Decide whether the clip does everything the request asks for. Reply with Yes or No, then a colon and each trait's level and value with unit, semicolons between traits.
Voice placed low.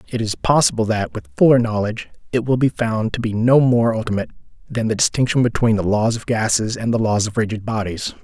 Yes: low, 115 Hz